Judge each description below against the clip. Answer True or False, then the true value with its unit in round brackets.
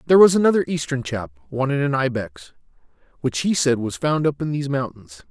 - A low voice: False (145 Hz)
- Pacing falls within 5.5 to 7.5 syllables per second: True (6.0 syllables/s)